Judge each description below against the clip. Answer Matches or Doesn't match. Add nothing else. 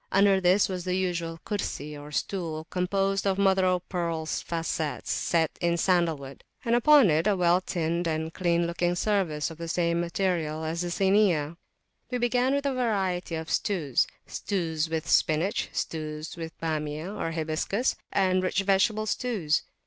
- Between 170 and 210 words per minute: Doesn't match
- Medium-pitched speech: Matches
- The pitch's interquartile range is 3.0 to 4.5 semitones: Matches